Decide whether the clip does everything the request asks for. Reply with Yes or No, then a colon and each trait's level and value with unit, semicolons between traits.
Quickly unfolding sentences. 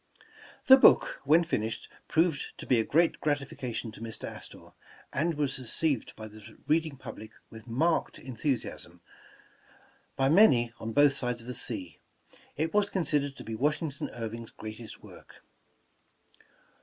No: average, 150 wpm